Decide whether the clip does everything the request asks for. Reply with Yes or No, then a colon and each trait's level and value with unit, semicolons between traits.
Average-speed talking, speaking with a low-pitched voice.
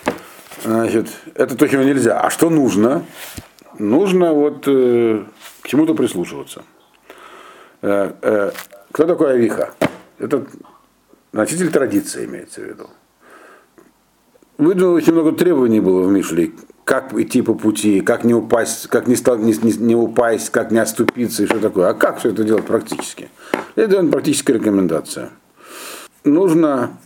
Yes: average, 140 wpm; low, 115 Hz